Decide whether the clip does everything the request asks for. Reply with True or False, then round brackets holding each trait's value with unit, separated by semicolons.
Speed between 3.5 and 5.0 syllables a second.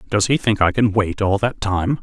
True (4.9 syllables/s)